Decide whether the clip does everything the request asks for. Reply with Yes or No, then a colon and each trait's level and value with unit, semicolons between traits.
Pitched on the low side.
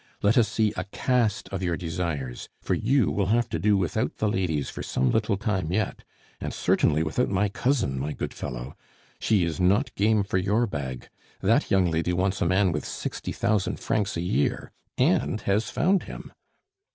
Yes: very low, 95 Hz